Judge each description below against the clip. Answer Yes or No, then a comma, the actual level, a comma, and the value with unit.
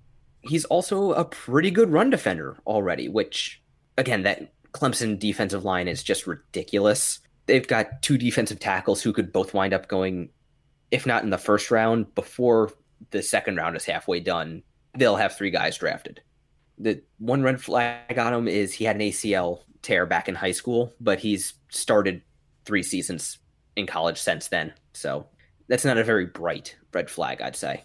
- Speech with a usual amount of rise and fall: Yes, average, 4.0 semitones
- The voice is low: Yes, low, 110 Hz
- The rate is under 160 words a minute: No, average, 175 wpm